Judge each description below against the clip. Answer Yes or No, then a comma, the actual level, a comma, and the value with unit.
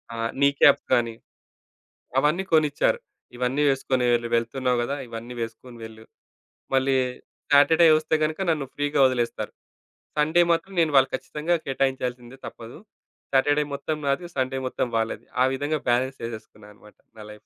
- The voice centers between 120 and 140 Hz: Yes, low, 135 Hz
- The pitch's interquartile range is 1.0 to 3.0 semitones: No, average, 3.8 semitones